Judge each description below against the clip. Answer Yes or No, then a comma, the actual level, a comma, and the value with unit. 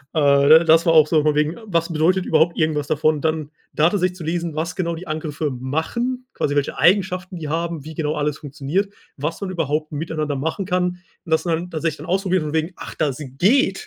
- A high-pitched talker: No, medium, 160 Hz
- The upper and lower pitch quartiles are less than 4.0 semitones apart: Yes, average, 2.8 semitones